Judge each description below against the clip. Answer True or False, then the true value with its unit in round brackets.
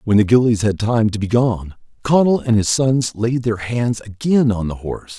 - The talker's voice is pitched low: True (115 Hz)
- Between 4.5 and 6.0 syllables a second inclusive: True (4.8 syllables/s)